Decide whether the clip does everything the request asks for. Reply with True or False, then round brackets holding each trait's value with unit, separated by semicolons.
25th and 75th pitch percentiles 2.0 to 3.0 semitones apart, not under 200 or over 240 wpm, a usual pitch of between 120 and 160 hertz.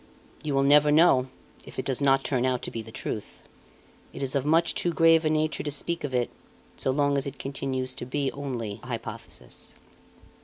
True (2.6 semitones; 205 wpm; 135 Hz)